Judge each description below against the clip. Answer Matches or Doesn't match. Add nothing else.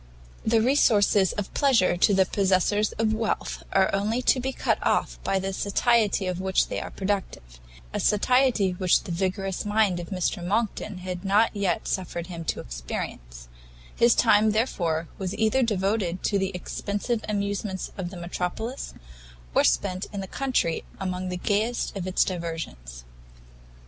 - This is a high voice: Matches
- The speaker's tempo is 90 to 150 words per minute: Doesn't match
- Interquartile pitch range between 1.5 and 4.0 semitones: Matches